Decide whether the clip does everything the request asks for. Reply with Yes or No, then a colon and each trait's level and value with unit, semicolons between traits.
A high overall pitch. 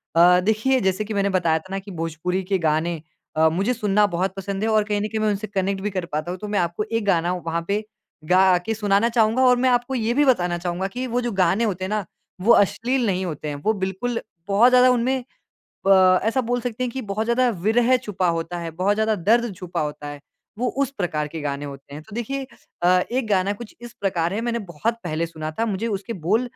Yes: high, 200 Hz